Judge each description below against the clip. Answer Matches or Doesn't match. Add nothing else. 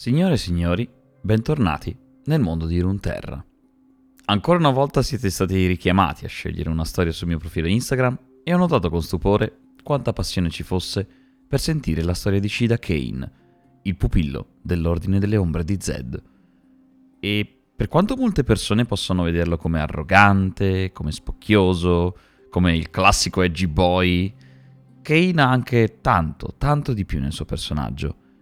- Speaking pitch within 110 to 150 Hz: Doesn't match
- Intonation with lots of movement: Matches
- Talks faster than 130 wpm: Matches